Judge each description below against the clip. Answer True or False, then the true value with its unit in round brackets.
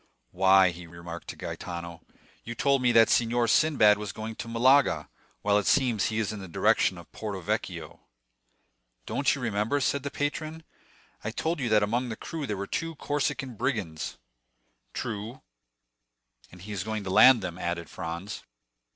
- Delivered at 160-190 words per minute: True (170 wpm)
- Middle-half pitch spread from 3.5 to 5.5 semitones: True (5.2 semitones)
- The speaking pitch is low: True (110 Hz)